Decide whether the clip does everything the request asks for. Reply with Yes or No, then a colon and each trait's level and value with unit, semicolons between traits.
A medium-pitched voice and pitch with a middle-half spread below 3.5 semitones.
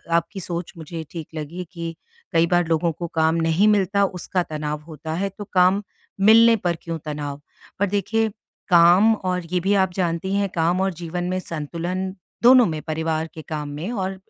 Yes: medium, 175 Hz; average, 2.9 semitones